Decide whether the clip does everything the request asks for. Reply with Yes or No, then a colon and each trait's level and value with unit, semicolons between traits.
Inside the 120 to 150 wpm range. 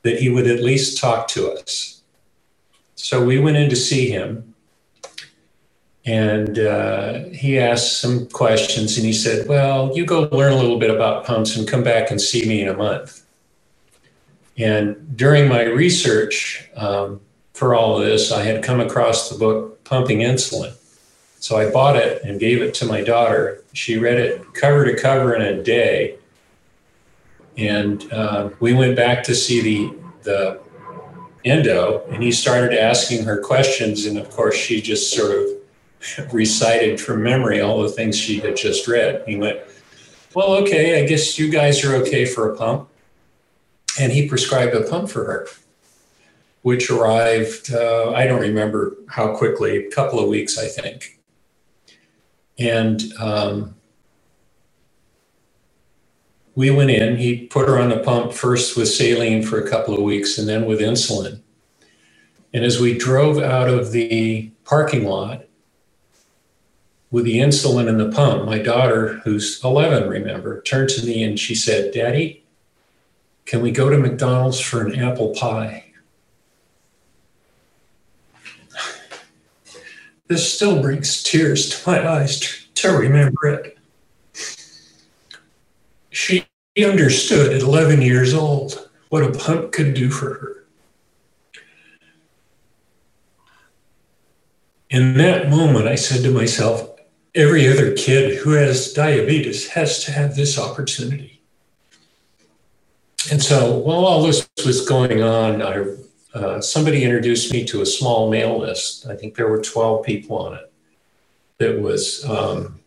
Yes: average, 145 wpm